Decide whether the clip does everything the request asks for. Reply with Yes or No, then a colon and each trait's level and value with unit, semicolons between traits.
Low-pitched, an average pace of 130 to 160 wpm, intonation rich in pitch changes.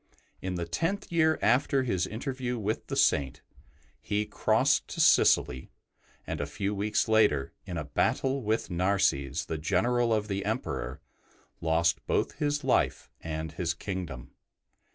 Yes: low, 100 Hz; average, 145 wpm; wide, 6.5 semitones